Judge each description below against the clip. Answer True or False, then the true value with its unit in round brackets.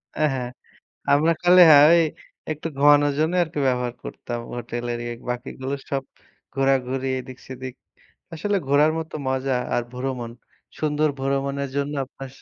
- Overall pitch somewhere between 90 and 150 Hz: True (135 Hz)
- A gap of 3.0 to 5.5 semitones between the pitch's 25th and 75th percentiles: False (2.6 semitones)